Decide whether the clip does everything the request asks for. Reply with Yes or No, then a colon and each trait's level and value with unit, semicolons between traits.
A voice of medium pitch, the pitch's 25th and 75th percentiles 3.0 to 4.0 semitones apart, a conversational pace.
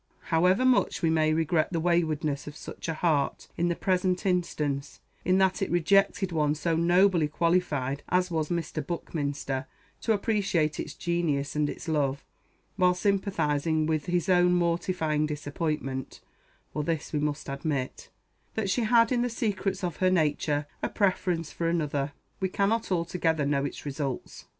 Yes: medium, 165 Hz; average, 3.5 semitones; average, 160 wpm